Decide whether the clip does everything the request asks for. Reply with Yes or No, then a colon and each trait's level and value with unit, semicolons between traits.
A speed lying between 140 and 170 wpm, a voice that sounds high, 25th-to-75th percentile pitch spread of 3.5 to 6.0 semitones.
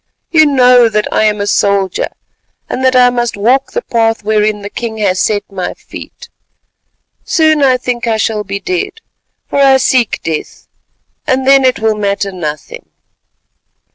Yes: average, 165 wpm; high, 225 Hz; average, 4.2 semitones